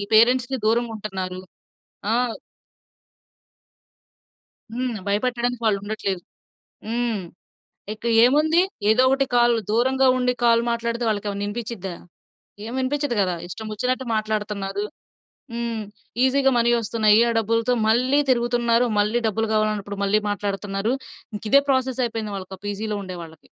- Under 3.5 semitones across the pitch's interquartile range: Yes, average, 3.0 semitones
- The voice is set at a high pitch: Yes, high, 225 Hz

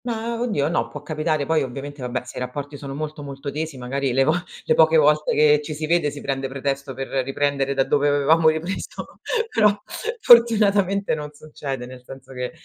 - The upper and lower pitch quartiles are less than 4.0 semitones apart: Yes, narrow, 2.6 semitones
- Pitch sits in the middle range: Yes, medium, 145 Hz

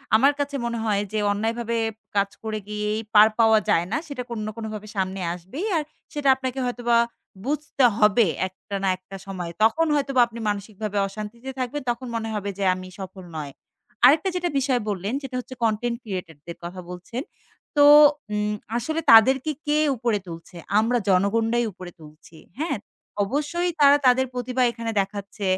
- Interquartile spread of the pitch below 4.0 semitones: No, average, 4.5 semitones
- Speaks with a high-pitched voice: Yes, high, 225 Hz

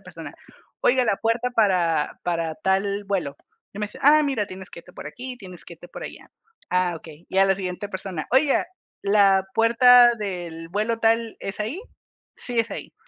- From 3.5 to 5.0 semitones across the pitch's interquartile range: Yes, average, 4.1 semitones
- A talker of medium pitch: No, high, 200 Hz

